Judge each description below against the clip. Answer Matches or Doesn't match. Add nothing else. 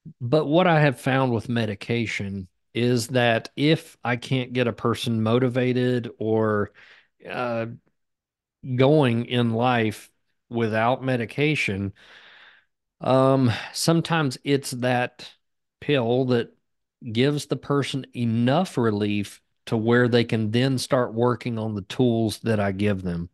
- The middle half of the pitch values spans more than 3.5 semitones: Doesn't match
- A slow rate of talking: Matches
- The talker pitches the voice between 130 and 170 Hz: Doesn't match